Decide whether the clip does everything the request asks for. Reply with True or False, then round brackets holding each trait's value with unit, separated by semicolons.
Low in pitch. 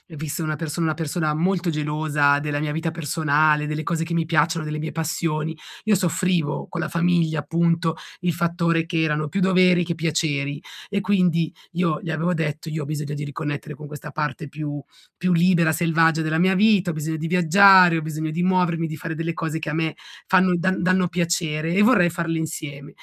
False (165 Hz)